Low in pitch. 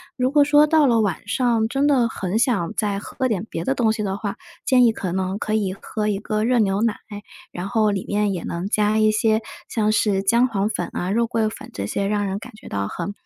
No: high, 215 Hz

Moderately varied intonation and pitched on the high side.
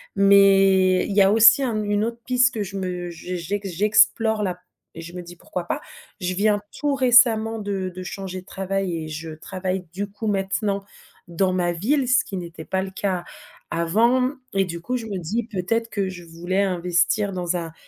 Yes: average, 3.0 semitones; high, 195 Hz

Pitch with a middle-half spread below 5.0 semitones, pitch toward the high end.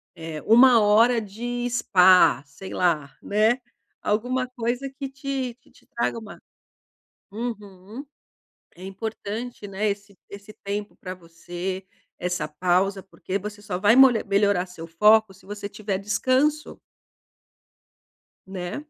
Yes: average, 4.1 semitones; high, 205 Hz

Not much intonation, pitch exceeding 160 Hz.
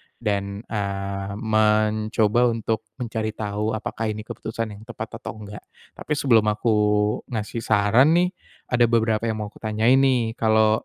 No: narrow, 1.5 semitones; low, 110 Hz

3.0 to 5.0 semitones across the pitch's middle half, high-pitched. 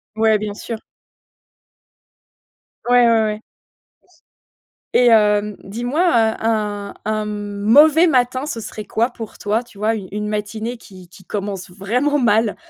No: narrow, 2.5 semitones; high, 215 Hz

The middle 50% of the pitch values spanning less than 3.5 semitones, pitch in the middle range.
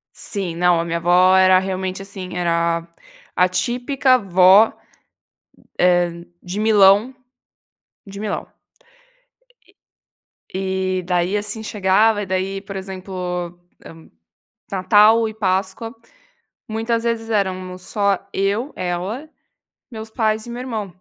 No: average, 3.0 semitones; high, 195 Hz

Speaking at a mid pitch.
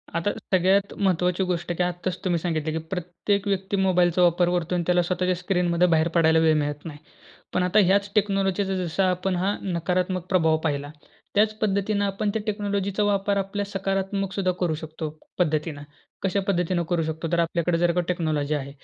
Yes: medium, 180 Hz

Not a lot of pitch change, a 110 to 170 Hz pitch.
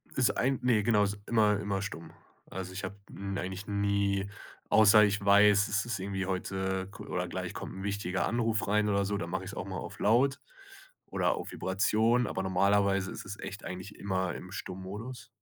No: narrow, 1.8 semitones; low, 100 Hz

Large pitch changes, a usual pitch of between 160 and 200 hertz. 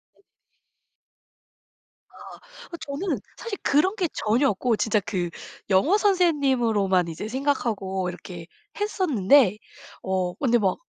No: wide, 8.5 semitones; high, 235 Hz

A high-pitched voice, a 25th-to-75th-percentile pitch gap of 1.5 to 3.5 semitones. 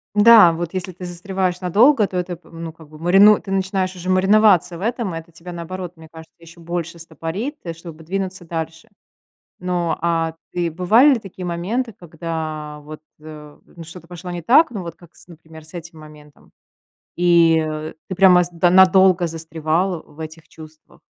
No: medium, 175 Hz; narrow, 2.5 semitones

